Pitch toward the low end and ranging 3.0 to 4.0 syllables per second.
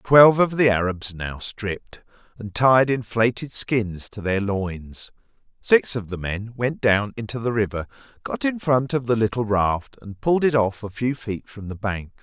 No: low, 110 Hz; 4.5 syllables/s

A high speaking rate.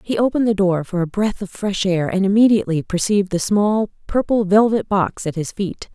Yes: fast, 210 wpm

